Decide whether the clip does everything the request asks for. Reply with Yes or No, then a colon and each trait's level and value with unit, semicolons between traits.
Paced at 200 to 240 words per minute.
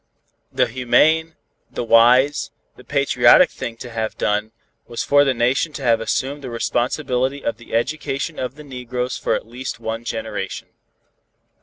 No: average, 155 wpm